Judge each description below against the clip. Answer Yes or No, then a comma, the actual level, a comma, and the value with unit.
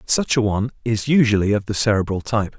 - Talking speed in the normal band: No, fast, 210 wpm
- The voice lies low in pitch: Yes, low, 110 Hz